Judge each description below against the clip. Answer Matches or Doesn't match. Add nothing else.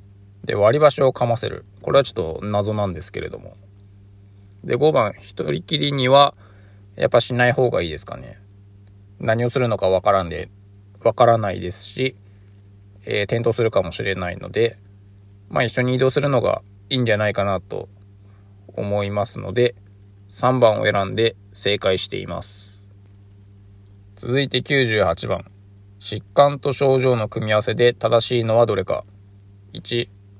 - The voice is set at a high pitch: Doesn't match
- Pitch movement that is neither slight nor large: Matches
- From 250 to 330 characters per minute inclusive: Matches